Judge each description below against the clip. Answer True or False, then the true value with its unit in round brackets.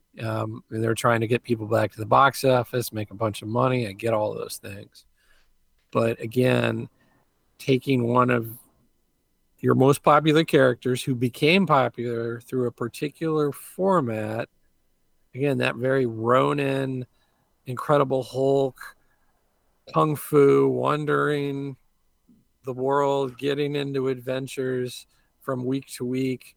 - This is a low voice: True (130 Hz)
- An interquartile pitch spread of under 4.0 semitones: True (2.9 semitones)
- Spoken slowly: True (125 wpm)